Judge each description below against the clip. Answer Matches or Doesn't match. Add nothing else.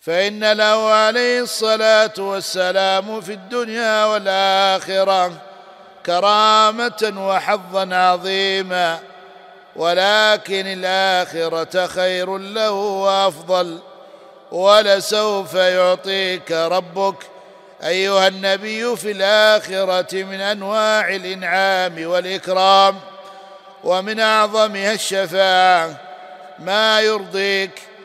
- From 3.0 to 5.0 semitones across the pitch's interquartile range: Doesn't match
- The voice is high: Matches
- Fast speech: Doesn't match